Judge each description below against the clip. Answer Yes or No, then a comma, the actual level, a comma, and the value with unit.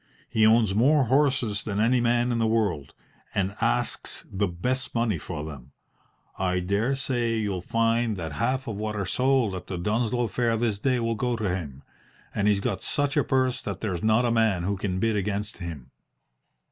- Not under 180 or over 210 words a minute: Yes, average, 195 wpm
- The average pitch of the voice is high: No, low, 110 Hz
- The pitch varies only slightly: No, average, 4.0 semitones